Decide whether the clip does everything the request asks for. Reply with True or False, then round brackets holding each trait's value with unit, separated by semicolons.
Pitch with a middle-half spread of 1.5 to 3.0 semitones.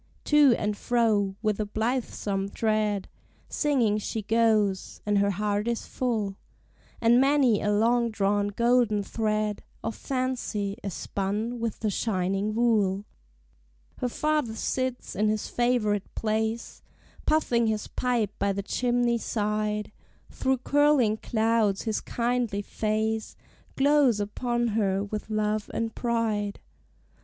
True (2.6 semitones)